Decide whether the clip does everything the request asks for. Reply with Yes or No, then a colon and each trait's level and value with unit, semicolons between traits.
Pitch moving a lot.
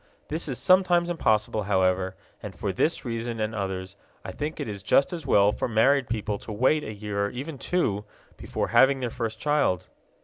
Yes: wide, 5.9 semitones